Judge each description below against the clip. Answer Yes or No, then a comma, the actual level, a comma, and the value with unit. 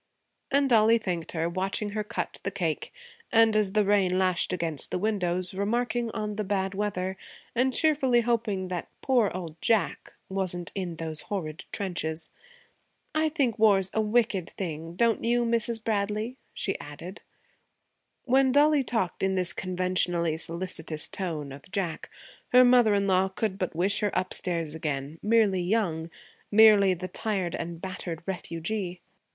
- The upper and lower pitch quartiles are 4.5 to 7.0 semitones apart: No, average, 3.9 semitones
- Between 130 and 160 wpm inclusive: Yes, average, 150 wpm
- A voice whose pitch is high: Yes, high, 195 Hz